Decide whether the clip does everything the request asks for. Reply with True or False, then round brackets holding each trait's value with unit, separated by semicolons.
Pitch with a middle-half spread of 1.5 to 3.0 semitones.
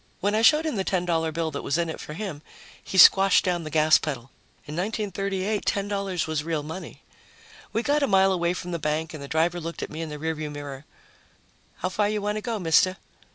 False (4.1 semitones)